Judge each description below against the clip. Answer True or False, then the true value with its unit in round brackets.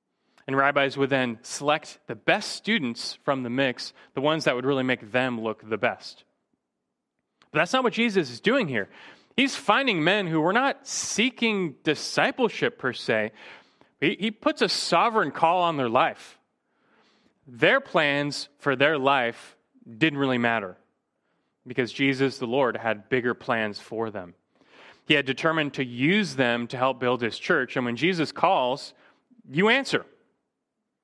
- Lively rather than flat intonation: True (7.4 semitones)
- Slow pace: False (155 wpm)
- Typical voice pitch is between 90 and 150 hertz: True (140 Hz)